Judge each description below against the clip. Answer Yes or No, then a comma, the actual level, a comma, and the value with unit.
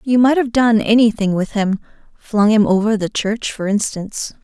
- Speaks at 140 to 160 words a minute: No, average, 175 wpm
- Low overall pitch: No, high, 215 Hz